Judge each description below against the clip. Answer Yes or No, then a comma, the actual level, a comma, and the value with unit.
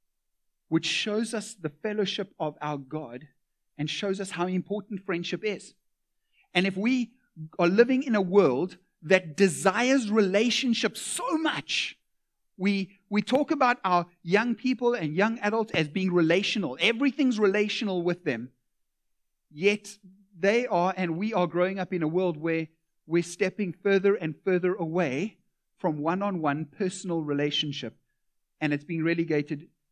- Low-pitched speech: No, medium, 185 Hz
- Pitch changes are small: No, average, 4.1 semitones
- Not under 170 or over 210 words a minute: No, average, 140 wpm